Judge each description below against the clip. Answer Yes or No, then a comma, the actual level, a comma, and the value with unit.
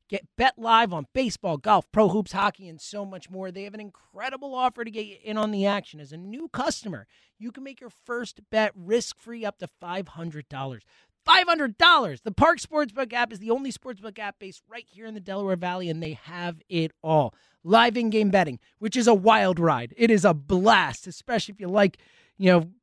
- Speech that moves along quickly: Yes, fast, 215 wpm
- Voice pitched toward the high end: Yes, high, 210 Hz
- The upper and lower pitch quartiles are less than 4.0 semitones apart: No, average, 4.6 semitones